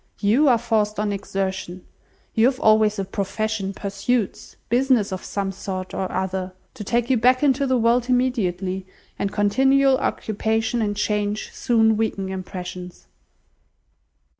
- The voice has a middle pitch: No, high, 210 Hz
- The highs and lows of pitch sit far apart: No, average, 3.8 semitones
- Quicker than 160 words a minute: No, average, 140 wpm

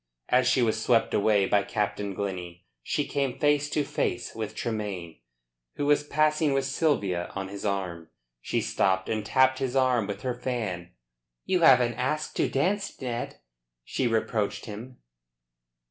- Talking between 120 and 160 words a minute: Yes, average, 155 wpm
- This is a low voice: Yes, low, 120 Hz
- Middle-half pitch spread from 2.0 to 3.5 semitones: No, average, 5.1 semitones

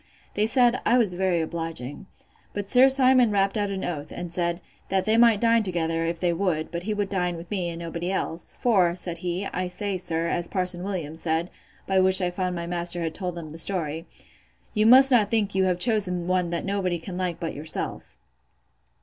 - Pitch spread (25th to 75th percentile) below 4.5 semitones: Yes, average, 3.0 semitones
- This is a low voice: No, medium, 180 Hz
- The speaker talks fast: Yes, fast, 210 wpm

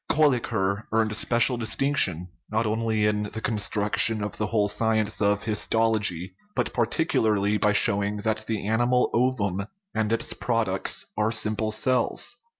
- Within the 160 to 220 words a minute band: No, average, 145 wpm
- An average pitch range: No, narrow, 1.8 semitones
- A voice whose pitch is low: Yes, low, 110 Hz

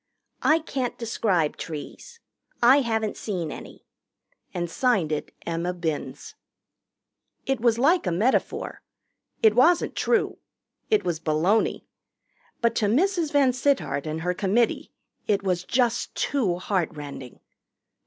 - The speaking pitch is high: Yes, high, 215 Hz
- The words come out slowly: Yes, slow, 125 wpm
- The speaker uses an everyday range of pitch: No, wide, 6.9 semitones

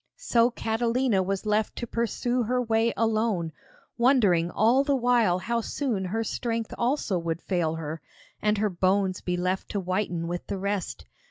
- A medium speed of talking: Yes, average, 165 wpm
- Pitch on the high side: Yes, high, 215 Hz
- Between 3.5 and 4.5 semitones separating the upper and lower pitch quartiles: Yes, average, 4.2 semitones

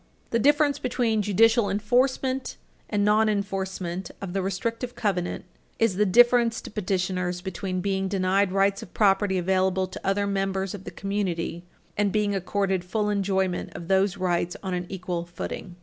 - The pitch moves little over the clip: Yes, narrow, 2.2 semitones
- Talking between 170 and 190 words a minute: No, average, 155 wpm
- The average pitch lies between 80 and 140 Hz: No, high, 195 Hz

